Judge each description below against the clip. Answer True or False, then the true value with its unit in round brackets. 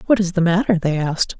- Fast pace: True (260 wpm)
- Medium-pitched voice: True (175 Hz)